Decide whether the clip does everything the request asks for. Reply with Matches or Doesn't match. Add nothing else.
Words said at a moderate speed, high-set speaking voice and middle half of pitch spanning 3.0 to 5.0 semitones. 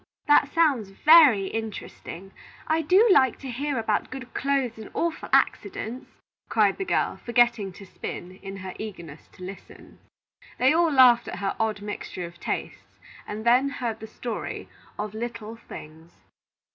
Doesn't match